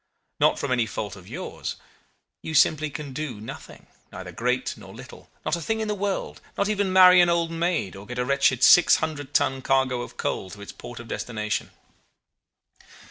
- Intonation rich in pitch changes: Yes, wide, 6.4 semitones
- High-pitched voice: No, low, 135 Hz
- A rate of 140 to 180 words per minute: No, average, 190 wpm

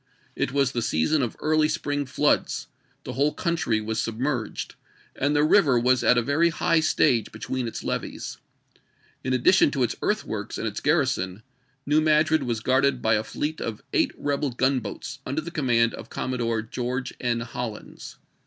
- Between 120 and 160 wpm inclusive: No, average, 170 wpm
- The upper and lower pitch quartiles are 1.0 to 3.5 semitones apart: No, average, 4.1 semitones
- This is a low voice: Yes, low, 130 Hz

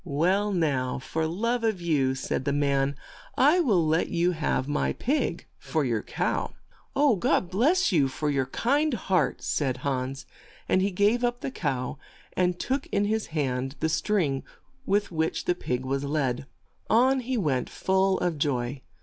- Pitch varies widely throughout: Yes, wide, 7.3 semitones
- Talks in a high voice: No, medium, 165 Hz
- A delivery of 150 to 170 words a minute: Yes, average, 165 wpm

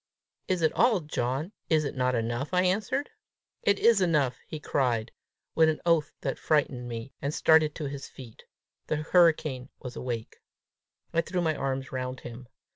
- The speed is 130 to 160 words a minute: No, average, 170 wpm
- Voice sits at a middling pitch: Yes, medium, 145 Hz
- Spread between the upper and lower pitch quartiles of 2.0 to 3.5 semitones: No, average, 4.6 semitones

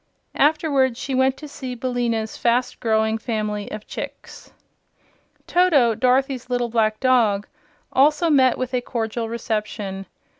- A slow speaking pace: Yes, slow, 125 wpm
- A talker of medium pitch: No, high, 245 Hz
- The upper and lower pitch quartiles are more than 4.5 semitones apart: No, average, 3.1 semitones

